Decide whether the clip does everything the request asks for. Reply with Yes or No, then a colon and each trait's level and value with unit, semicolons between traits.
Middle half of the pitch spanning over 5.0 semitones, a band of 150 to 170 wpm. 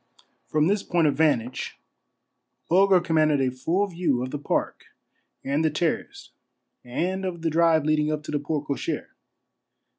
No: average, 3.0 semitones; average, 160 wpm